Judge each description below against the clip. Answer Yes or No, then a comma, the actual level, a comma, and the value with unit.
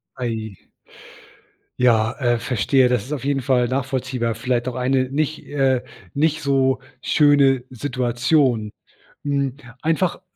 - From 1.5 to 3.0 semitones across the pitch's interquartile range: Yes, narrow, 2.4 semitones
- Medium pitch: No, low, 130 Hz